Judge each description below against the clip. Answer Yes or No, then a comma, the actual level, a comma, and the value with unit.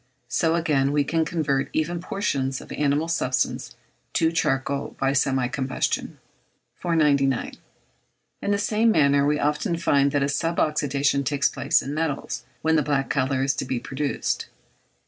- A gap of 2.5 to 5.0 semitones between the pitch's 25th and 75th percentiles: Yes, average, 2.9 semitones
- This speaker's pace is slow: No, average, 155 wpm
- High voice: No, medium, 145 Hz